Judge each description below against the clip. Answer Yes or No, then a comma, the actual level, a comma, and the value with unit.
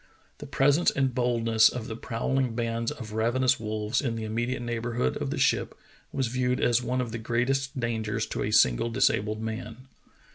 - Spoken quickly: No, average, 190 wpm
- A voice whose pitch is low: Yes, low, 120 Hz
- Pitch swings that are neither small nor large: No, narrow, 2.2 semitones